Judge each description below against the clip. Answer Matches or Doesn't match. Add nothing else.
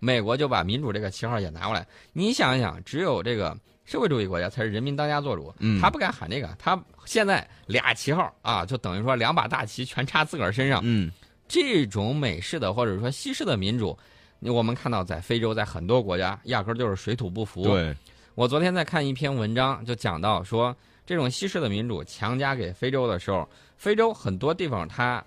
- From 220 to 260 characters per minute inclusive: Doesn't match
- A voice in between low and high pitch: Doesn't match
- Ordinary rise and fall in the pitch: Matches